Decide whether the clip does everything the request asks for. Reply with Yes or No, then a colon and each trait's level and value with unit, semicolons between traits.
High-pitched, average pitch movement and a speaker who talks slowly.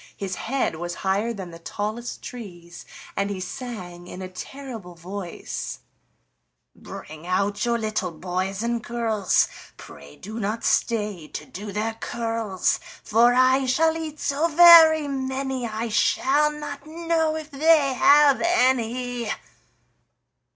No: high, 230 Hz; wide, 5.9 semitones; slow, 130 wpm